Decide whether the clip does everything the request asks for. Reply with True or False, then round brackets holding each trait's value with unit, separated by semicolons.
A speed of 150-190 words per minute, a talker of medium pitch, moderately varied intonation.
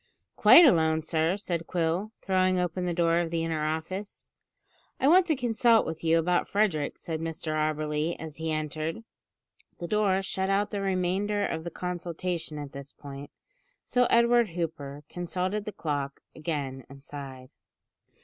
True (160 wpm; 170 Hz; 3.8 semitones)